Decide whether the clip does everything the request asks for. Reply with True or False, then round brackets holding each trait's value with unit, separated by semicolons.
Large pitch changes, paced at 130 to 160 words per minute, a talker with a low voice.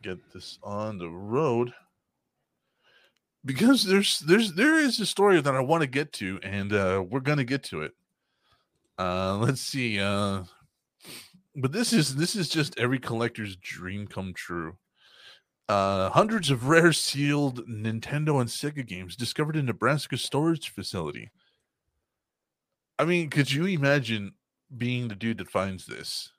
True (7.2 semitones; 150 wpm; 130 Hz)